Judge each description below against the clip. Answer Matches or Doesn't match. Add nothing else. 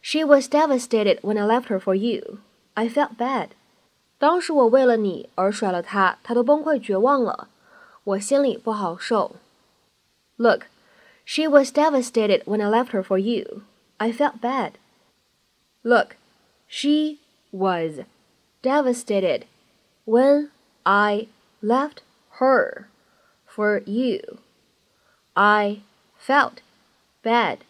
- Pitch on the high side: Matches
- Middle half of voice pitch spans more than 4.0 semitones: Matches